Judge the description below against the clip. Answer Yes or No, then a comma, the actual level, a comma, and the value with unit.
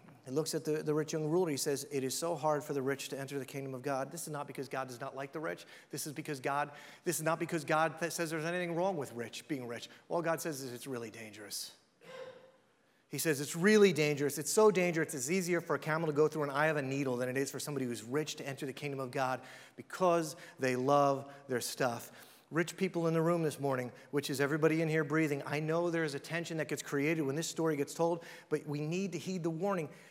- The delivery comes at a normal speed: No, fast, 255 wpm